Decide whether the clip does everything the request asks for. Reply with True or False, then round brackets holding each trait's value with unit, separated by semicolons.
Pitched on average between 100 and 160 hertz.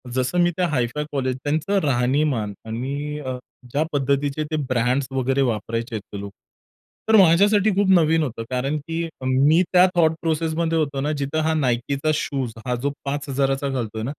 True (140 Hz)